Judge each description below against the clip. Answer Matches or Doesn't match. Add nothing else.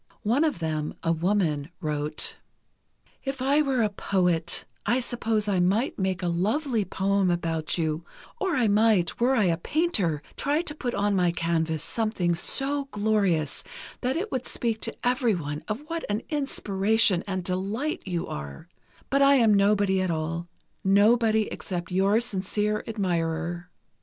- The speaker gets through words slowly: Doesn't match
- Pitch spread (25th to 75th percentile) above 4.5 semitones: Matches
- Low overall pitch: Doesn't match